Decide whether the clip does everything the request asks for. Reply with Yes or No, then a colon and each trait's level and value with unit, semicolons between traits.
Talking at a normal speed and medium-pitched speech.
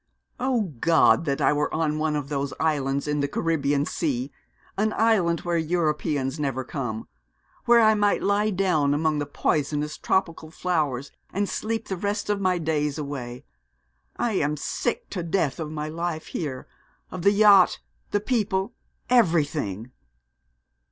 Yes: average, 150 wpm; medium, 160 Hz